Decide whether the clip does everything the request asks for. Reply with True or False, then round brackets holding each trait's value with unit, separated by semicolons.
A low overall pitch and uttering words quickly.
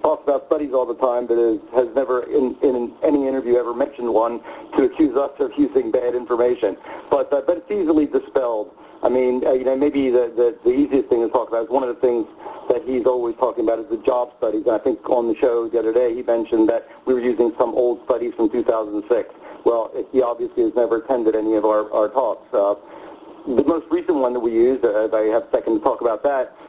True (130 Hz; 245 wpm)